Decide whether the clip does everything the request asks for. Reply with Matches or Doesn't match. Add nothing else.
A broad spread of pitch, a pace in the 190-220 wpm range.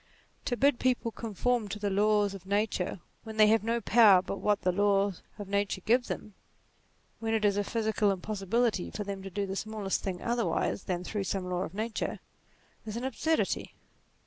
Doesn't match